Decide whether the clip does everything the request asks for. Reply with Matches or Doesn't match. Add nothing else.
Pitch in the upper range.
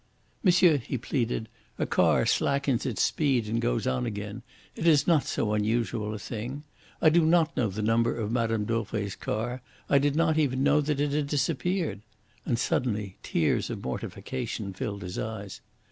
Doesn't match